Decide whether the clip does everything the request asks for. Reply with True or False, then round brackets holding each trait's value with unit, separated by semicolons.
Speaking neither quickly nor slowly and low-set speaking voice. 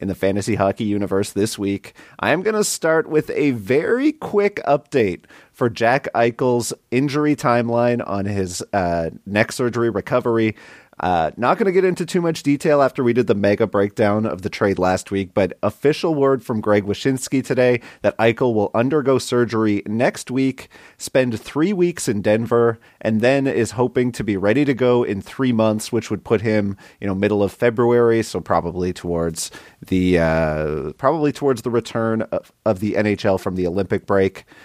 True (180 wpm; 115 Hz)